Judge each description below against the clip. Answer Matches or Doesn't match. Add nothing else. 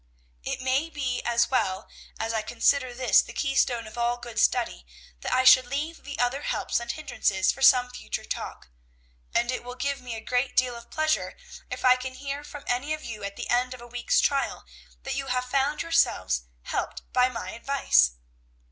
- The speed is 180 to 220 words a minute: Matches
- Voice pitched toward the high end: Matches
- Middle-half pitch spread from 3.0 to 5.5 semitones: Doesn't match